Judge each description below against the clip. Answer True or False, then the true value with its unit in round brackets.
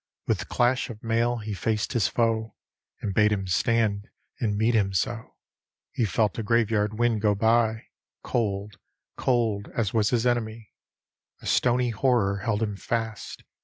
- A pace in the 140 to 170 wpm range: True (155 wpm)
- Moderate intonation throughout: False (2.2 semitones)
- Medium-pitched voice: False (110 Hz)